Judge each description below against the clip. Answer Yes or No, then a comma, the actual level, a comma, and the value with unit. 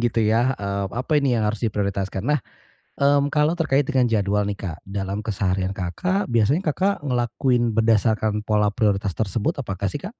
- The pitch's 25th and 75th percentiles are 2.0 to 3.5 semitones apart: No, wide, 5.6 semitones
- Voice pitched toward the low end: Yes, low, 110 Hz